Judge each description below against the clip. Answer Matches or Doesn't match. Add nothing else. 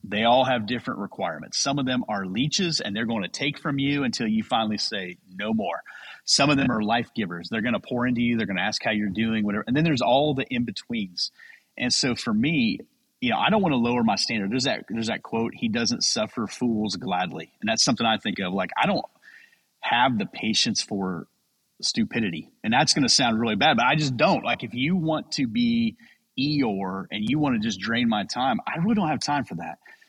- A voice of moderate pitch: Matches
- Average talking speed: Doesn't match